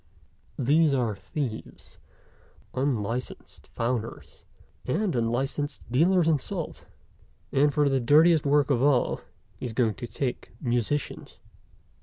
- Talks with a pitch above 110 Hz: Yes, low, 135 Hz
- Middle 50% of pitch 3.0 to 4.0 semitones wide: Yes, average, 3.6 semitones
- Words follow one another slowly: Yes, slow, 115 wpm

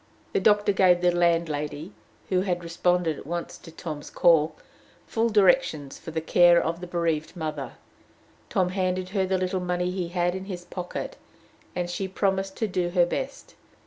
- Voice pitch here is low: No, medium, 180 Hz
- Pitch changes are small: Yes, narrow, 2.0 semitones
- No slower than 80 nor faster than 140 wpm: No, average, 175 wpm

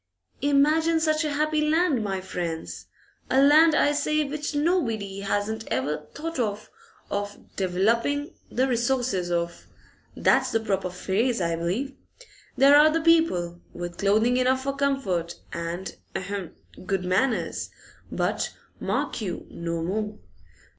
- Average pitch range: No, wide, 7.8 semitones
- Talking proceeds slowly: Yes, slow, 130 wpm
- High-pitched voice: Yes, high, 225 Hz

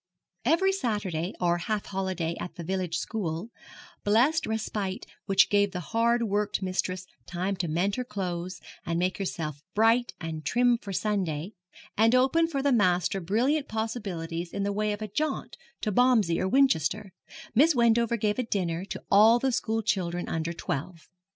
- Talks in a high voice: Yes, high, 200 Hz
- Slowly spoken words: No, average, 165 wpm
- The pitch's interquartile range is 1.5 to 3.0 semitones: No, average, 4.6 semitones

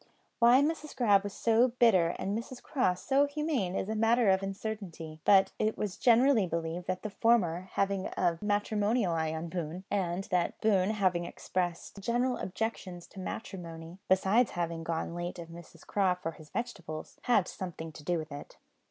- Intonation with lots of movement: No, average, 4.5 semitones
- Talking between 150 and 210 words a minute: Yes, average, 180 wpm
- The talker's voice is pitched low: No, high, 190 Hz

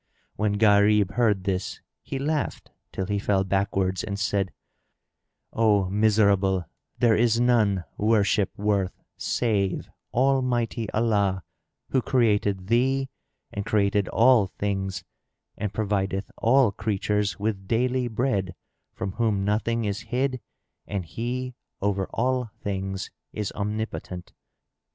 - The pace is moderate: No, slow, 115 wpm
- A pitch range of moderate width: Yes, average, 3.1 semitones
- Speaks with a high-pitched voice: No, low, 105 Hz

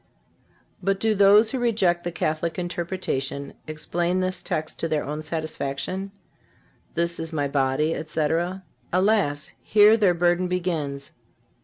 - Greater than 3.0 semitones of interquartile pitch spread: Yes, average, 3.5 semitones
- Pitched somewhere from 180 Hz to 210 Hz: No, medium, 170 Hz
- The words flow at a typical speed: No, slow, 130 wpm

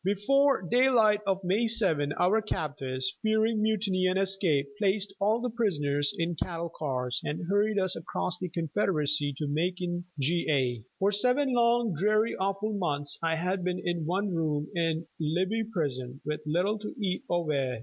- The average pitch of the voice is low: No, medium, 180 Hz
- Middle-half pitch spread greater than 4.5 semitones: Yes, wide, 5.5 semitones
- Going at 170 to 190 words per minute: No, average, 160 wpm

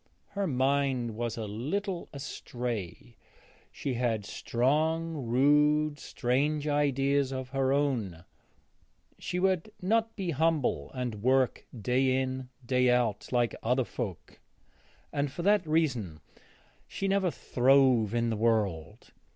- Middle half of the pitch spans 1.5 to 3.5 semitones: No, average, 4.1 semitones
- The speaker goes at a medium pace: No, slow, 120 wpm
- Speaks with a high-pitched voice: No, low, 130 Hz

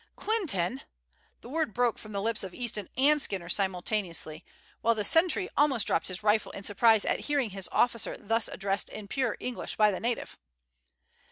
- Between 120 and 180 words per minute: Yes, average, 175 wpm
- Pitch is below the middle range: No, high, 215 Hz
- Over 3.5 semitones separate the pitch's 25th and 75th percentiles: Yes, average, 4.0 semitones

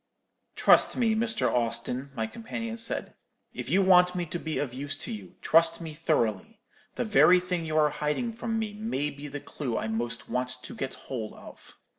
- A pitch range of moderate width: No, wide, 8.1 semitones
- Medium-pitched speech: Yes, medium, 165 Hz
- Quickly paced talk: No, average, 195 wpm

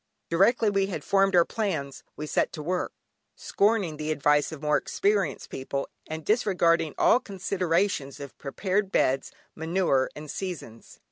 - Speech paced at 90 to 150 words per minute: Yes, average, 145 wpm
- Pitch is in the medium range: Yes, medium, 170 Hz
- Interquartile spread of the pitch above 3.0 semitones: Yes, average, 4.7 semitones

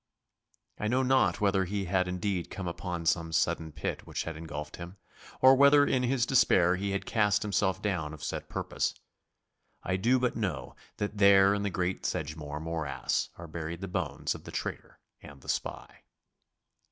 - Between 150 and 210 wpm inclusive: Yes, average, 175 wpm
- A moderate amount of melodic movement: Yes, average, 3.8 semitones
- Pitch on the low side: Yes, very low, 95 Hz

